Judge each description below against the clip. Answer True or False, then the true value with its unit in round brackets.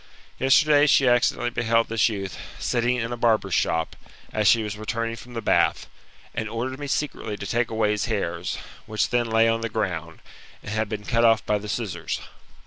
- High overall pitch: False (115 Hz)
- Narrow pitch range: True (2.2 semitones)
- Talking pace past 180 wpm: True (195 wpm)